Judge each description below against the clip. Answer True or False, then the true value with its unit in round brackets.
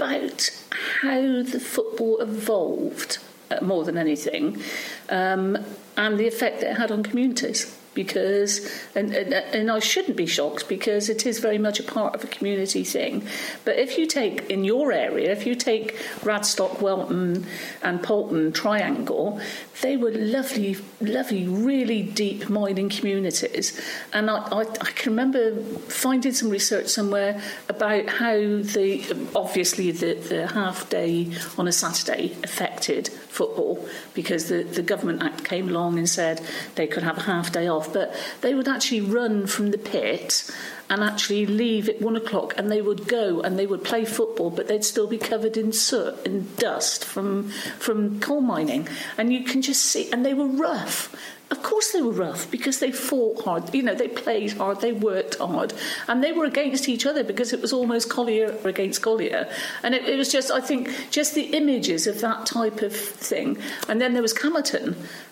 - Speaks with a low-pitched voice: False (220 Hz)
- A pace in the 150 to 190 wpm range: True (175 wpm)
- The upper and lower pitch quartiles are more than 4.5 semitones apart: False (3.8 semitones)